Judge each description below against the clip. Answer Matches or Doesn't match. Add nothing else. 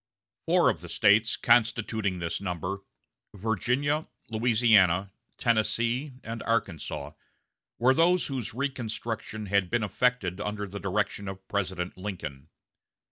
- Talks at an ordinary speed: Doesn't match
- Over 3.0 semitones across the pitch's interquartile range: Matches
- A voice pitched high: Doesn't match